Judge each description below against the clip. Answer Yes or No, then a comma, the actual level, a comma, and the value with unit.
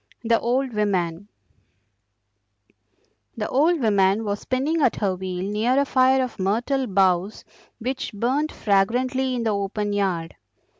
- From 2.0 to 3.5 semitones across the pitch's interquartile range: No, average, 4.7 semitones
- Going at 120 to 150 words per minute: Yes, slow, 135 wpm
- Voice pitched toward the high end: Yes, high, 220 Hz